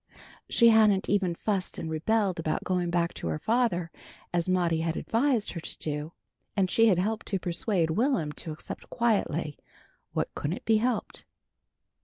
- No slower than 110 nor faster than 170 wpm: Yes, average, 165 wpm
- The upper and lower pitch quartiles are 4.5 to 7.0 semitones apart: Yes, average, 5.0 semitones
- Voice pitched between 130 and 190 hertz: Yes, medium, 185 Hz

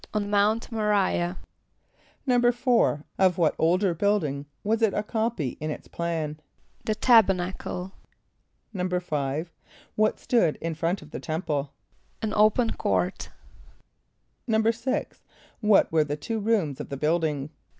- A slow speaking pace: Yes, slow, 130 wpm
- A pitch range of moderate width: No, wide, 5.7 semitones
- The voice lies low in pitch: No, medium, 185 Hz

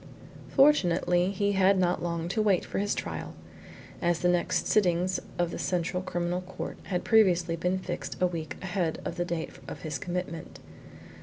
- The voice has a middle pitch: Yes, medium, 180 Hz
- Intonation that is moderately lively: No, narrow, 1.6 semitones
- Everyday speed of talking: Yes, average, 170 wpm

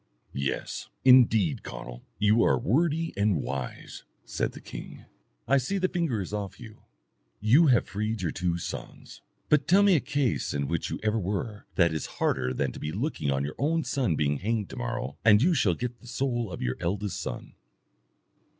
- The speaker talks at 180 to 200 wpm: Yes, average, 185 wpm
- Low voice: Yes, low, 110 Hz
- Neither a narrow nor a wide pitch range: No, wide, 7.2 semitones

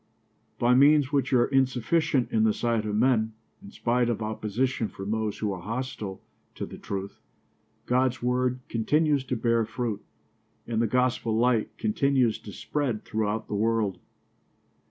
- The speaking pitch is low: Yes, low, 115 Hz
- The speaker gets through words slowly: No, average, 155 wpm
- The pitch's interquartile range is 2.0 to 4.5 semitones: Yes, average, 2.9 semitones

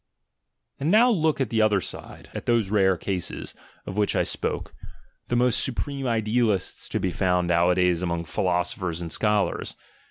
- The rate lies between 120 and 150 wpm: No, average, 160 wpm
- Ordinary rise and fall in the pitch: Yes, average, 4.9 semitones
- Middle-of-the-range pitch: No, low, 100 Hz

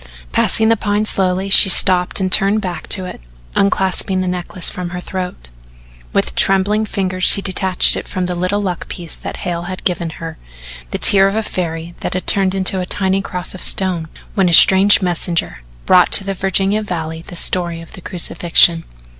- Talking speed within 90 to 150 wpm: No, average, 190 wpm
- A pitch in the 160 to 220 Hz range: Yes, medium, 185 Hz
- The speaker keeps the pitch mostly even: Yes, narrow, 1.8 semitones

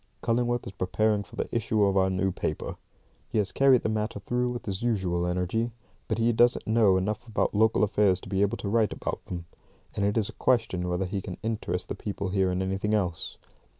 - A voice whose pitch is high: No, low, 105 Hz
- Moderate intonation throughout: Yes, average, 3.0 semitones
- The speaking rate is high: Yes, fast, 220 wpm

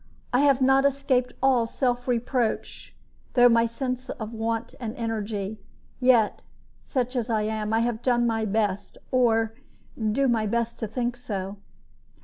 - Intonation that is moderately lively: No, narrow, 2.3 semitones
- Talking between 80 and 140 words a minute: No, average, 155 wpm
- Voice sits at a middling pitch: No, high, 235 Hz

